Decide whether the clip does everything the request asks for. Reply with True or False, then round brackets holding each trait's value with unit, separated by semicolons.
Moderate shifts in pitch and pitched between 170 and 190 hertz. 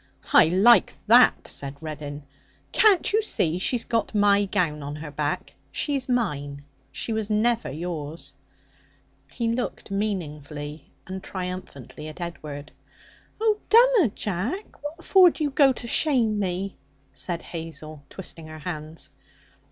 False (7.7 semitones; 185 Hz)